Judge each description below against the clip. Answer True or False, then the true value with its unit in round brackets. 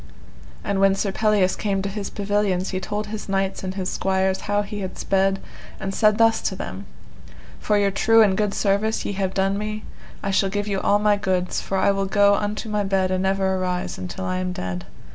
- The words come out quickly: True (220 wpm)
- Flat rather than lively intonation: True (1.4 semitones)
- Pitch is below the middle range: False (195 Hz)